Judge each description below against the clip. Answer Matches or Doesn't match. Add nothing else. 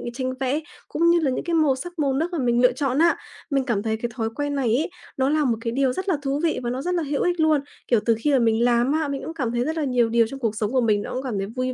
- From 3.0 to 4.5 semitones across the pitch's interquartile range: Matches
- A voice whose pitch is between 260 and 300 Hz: Matches